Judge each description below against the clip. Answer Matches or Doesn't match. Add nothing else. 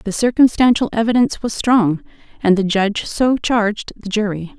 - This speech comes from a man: Doesn't match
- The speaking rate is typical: Matches